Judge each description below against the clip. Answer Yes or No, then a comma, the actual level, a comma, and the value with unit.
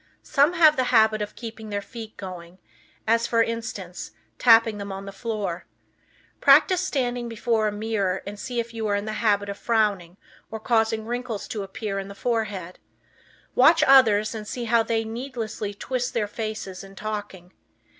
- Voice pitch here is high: Yes, high, 220 Hz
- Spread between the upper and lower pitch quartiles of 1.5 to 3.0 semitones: Yes, narrow, 2.5 semitones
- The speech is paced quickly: No, average, 175 wpm